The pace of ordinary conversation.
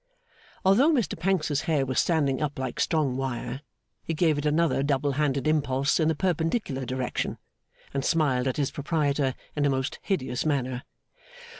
Yes: average, 160 wpm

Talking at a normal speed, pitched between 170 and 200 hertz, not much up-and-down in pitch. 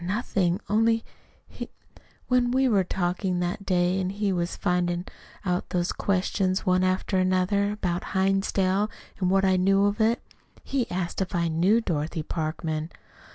Yes: average, 155 wpm; medium, 185 Hz; narrow, 2.3 semitones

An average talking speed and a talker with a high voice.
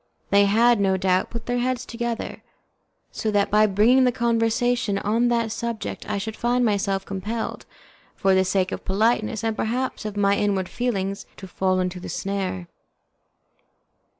Yes: average, 160 wpm; high, 210 Hz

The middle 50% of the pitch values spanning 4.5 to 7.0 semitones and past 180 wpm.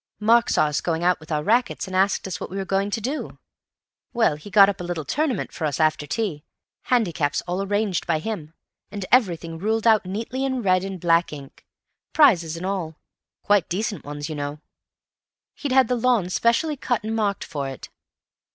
Yes: wide, 5.6 semitones; average, 190 wpm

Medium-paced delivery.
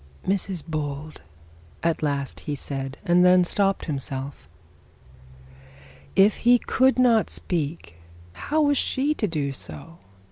No: slow, 130 wpm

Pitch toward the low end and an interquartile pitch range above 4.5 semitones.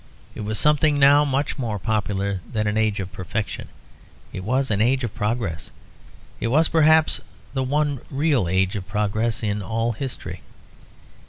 Yes: low, 110 Hz; average, 5.2 semitones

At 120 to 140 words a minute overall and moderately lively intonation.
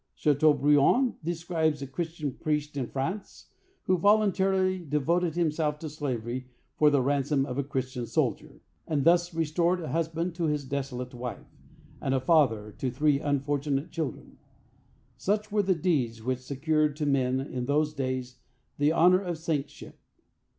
No: average, 150 wpm; average, 3.7 semitones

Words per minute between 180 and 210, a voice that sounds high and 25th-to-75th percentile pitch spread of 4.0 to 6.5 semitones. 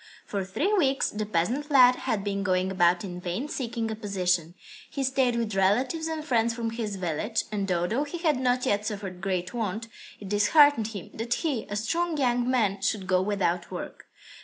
Yes: average, 190 wpm; high, 215 Hz; average, 4.8 semitones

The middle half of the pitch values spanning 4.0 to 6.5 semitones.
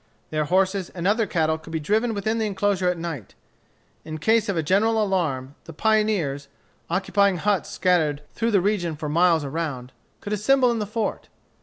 Yes: average, 4.9 semitones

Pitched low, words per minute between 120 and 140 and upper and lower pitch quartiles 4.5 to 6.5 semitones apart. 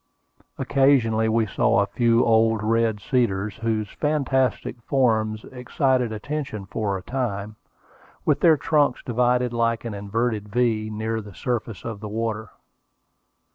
No: low, 115 Hz; slow, 135 wpm; narrow, 2.6 semitones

